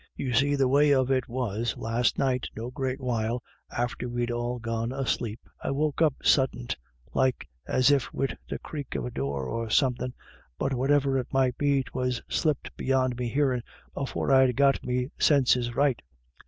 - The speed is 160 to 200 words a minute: Yes, average, 180 wpm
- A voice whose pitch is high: No, low, 125 Hz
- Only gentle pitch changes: Yes, narrow, 2.1 semitones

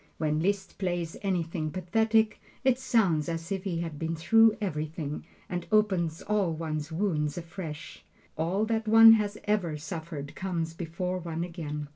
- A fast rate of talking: No, average, 150 wpm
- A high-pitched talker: No, medium, 170 Hz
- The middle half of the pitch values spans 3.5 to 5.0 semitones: Yes, average, 4.3 semitones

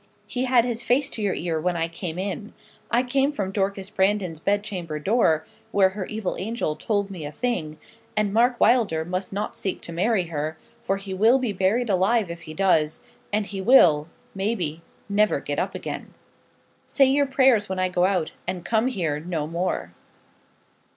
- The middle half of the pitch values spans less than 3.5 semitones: No, average, 4.8 semitones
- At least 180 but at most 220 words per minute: Yes, average, 185 wpm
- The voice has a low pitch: No, high, 195 Hz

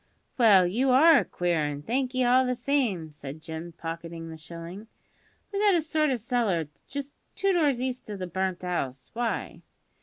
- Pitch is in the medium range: No, high, 210 Hz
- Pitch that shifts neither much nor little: No, wide, 7.7 semitones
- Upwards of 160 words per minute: Yes, average, 180 wpm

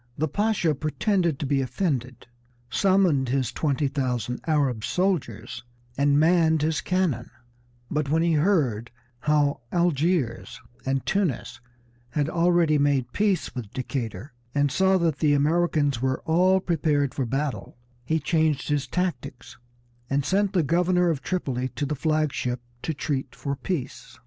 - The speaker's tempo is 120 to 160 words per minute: Yes, average, 145 wpm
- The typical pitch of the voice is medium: Yes, medium, 150 Hz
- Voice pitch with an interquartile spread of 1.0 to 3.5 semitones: No, average, 4.4 semitones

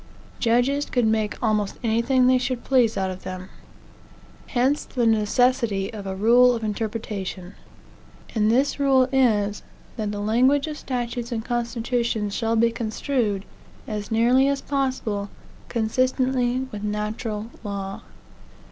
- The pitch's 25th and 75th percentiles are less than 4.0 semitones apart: Yes, average, 3.2 semitones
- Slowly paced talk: Yes, slow, 130 wpm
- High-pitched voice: Yes, high, 230 Hz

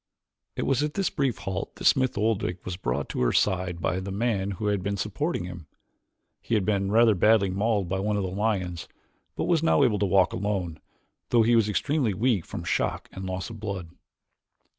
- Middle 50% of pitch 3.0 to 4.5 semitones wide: Yes, average, 3.4 semitones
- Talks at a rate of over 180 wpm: Yes, fast, 205 wpm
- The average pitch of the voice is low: Yes, low, 100 Hz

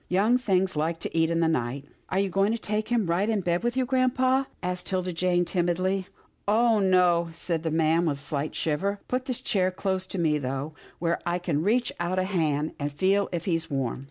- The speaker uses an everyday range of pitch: Yes, average, 3.6 semitones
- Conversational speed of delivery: No, fast, 240 wpm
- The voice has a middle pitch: Yes, medium, 180 Hz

